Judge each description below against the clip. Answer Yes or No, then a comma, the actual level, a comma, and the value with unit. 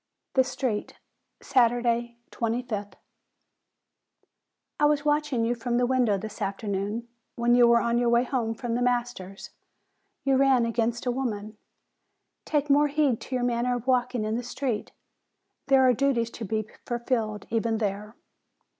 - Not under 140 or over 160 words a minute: Yes, average, 150 wpm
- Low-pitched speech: No, high, 240 Hz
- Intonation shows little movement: Yes, narrow, 2.2 semitones